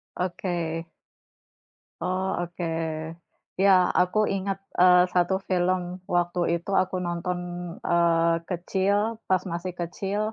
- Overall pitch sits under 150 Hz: No, medium, 180 Hz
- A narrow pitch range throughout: Yes, narrow, 1.6 semitones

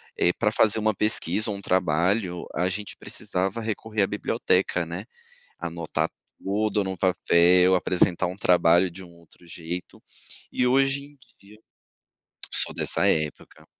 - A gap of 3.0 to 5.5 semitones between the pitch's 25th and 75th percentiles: Yes, average, 3.4 semitones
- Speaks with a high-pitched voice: No, very low, 95 Hz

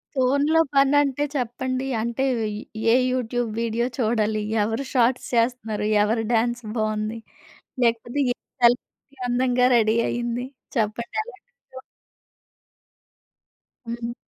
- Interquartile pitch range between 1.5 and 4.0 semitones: Yes, narrow, 2.4 semitones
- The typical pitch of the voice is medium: No, high, 240 Hz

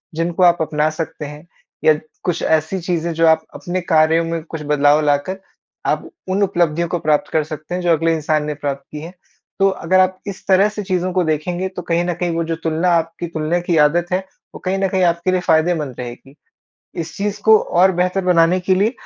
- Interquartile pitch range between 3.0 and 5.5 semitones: No, narrow, 2.6 semitones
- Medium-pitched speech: Yes, medium, 170 Hz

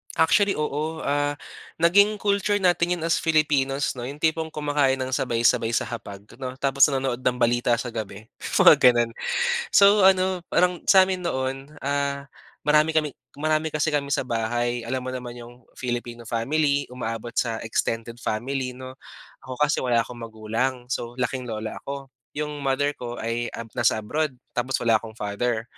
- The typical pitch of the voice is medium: No, low, 130 Hz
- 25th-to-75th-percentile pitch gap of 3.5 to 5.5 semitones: Yes, average, 4.1 semitones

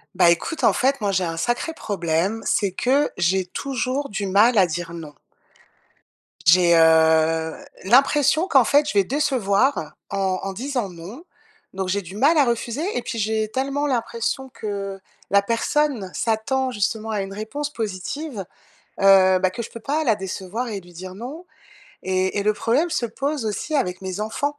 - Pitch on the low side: No, high, 215 Hz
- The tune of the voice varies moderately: No, wide, 5.9 semitones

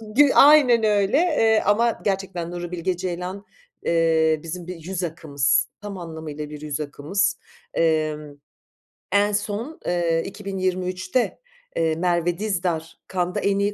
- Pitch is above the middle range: No, medium, 180 Hz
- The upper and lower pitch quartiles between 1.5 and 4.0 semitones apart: Yes, average, 3.7 semitones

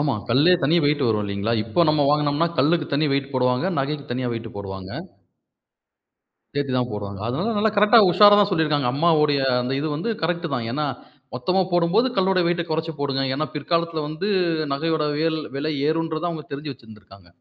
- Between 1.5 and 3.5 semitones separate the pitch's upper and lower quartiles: No, average, 4.6 semitones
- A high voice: No, medium, 150 Hz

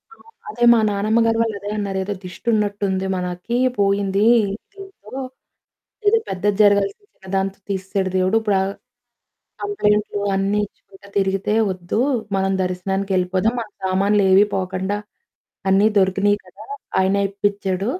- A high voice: Yes, high, 200 Hz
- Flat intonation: Yes, narrow, 1.6 semitones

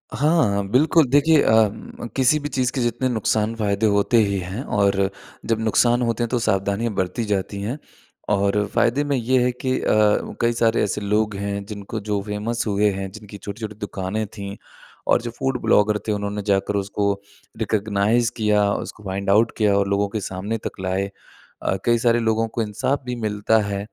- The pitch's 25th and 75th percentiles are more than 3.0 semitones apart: No, average, 2.7 semitones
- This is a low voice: Yes, low, 105 Hz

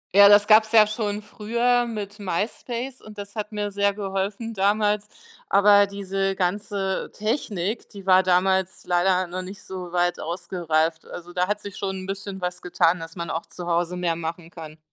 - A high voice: Yes, high, 195 Hz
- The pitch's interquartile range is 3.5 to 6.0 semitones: No, narrow, 2.6 semitones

